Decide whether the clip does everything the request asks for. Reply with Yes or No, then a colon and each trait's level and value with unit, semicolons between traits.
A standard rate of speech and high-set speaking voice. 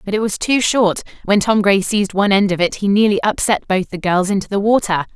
No: fast, 255 wpm; high, 200 Hz